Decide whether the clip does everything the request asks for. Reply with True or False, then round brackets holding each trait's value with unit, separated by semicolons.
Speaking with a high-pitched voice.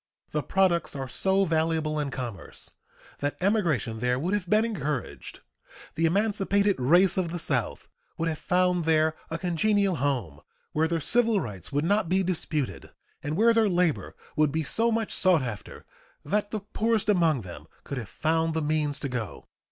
False (165 Hz)